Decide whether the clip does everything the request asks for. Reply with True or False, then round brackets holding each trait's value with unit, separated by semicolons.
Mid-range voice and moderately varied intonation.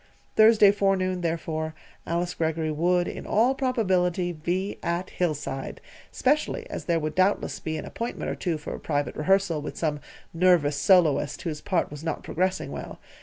True (175 Hz; 3.2 semitones)